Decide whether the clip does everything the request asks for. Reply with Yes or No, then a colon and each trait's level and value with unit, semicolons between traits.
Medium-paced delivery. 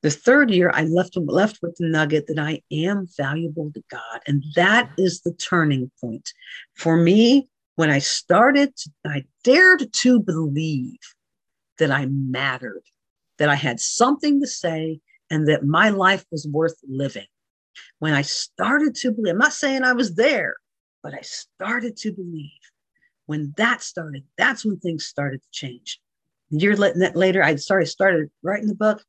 Yes: average, 165 wpm